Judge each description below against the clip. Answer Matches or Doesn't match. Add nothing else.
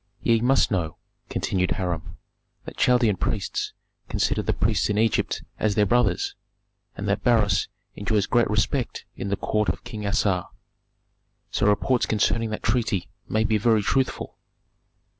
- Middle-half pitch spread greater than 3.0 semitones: Doesn't match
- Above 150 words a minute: Doesn't match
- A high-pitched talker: Doesn't match